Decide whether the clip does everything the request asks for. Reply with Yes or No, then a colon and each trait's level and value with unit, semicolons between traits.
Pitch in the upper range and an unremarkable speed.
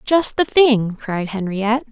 Yes: high, 230 Hz; average, 155 wpm